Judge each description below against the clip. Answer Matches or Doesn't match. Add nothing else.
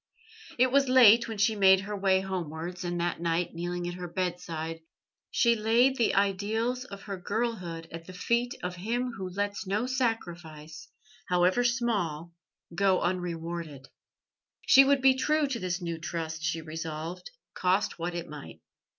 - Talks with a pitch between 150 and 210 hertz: Matches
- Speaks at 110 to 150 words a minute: Doesn't match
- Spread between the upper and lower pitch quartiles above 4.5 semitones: Matches